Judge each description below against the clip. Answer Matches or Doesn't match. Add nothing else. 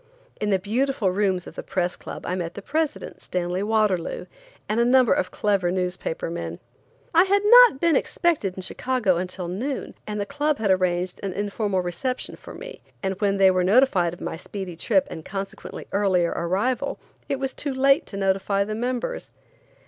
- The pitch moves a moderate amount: Doesn't match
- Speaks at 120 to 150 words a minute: Doesn't match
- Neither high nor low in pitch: Doesn't match